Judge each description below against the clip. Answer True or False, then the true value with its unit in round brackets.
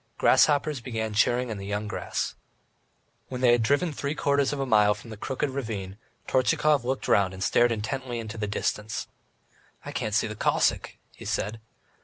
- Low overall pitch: True (115 Hz)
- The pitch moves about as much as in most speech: True (4.0 semitones)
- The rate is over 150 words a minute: True (180 wpm)